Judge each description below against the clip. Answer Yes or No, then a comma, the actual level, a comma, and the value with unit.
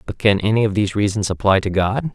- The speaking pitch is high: No, low, 105 Hz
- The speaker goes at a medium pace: No, fast, 250 wpm